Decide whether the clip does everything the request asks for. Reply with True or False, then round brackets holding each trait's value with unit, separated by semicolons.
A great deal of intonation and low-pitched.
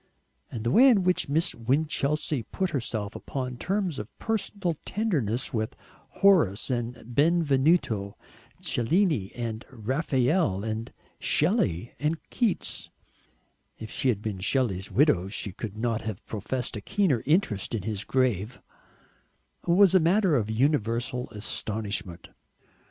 True (6.9 semitones; 125 Hz)